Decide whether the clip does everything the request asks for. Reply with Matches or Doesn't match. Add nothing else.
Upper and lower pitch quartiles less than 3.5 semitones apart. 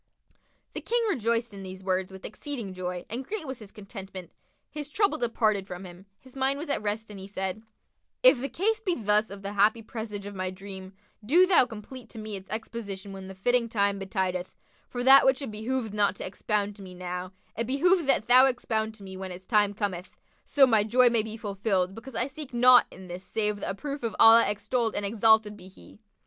Doesn't match